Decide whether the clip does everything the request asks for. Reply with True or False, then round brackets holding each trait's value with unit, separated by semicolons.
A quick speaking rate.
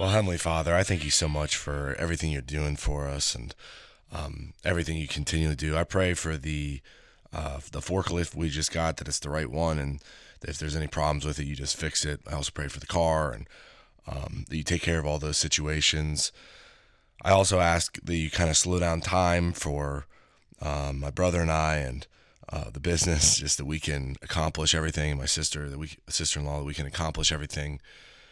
True (215 wpm)